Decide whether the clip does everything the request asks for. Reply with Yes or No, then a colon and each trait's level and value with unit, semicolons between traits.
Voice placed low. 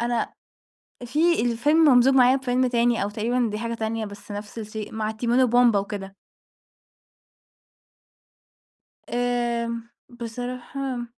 No: high, 235 Hz